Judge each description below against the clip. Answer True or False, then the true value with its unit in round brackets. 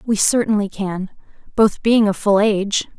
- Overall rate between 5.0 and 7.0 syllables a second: False (4.6 syllables/s)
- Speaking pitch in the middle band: False (205 Hz)